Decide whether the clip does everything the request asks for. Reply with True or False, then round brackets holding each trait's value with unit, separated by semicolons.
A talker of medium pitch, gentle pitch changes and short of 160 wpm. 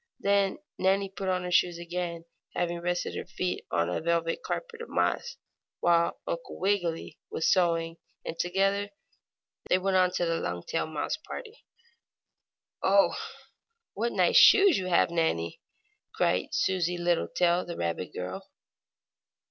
True (175 Hz; 2.3 semitones; 140 wpm)